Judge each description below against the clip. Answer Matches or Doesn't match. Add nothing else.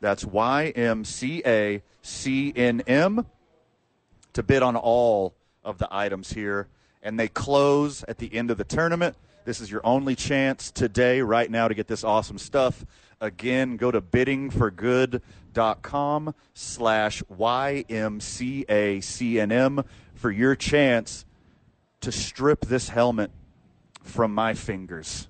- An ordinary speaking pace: Doesn't match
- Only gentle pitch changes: Doesn't match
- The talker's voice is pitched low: Matches